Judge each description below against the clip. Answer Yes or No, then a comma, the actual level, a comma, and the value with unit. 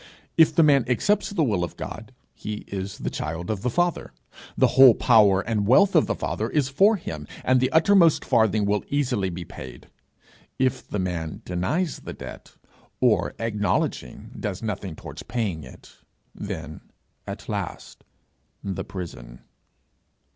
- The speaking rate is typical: Yes, average, 155 wpm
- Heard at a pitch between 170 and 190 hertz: No, low, 110 Hz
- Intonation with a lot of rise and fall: Yes, wide, 7.4 semitones